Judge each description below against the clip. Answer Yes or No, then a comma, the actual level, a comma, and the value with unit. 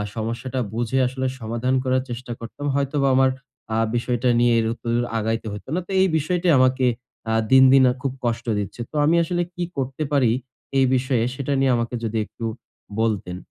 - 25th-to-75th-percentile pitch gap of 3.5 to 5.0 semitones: No, average, 2.7 semitones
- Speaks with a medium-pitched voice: No, low, 130 Hz